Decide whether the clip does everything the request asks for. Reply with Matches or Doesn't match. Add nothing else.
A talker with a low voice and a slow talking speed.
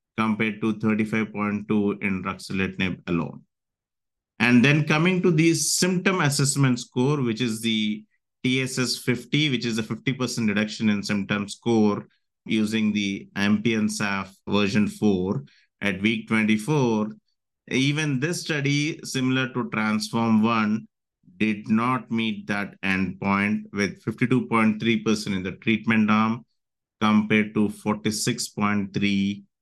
Matches